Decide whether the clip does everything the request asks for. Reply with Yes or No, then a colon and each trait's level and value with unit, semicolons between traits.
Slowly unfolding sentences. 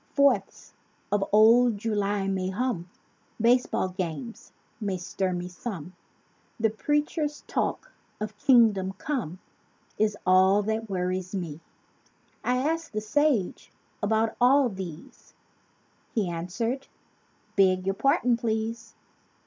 Yes: slow, 110 wpm